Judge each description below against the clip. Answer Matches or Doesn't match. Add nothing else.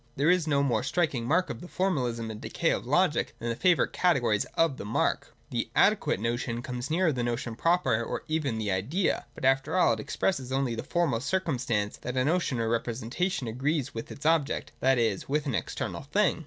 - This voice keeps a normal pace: Doesn't match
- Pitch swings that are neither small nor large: Doesn't match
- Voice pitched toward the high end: Doesn't match